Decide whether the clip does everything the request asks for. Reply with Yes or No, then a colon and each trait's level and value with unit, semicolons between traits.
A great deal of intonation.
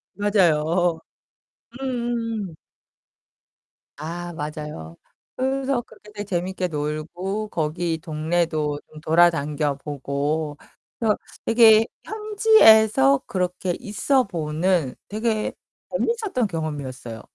Yes: wide, 6.2 semitones